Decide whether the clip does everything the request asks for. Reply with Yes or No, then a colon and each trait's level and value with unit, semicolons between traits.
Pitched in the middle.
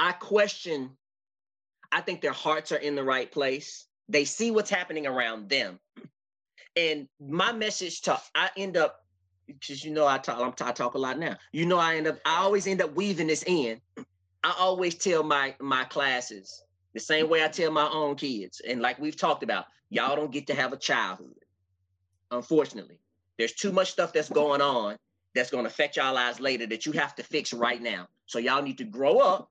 Yes: medium, 145 Hz